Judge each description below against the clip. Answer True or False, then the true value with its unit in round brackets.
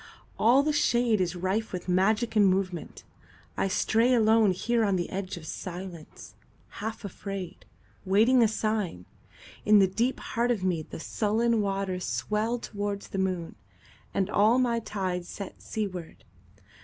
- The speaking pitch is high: True (200 Hz)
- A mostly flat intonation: False (3.3 semitones)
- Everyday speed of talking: False (130 wpm)